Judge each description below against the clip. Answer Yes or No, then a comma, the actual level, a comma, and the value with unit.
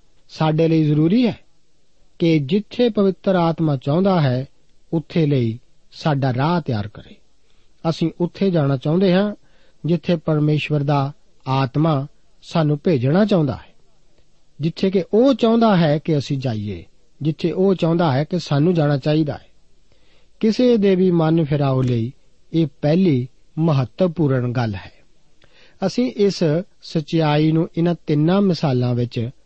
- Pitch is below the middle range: No, medium, 160 Hz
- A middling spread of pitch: Yes, average, 4.0 semitones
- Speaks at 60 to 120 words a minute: No, average, 130 wpm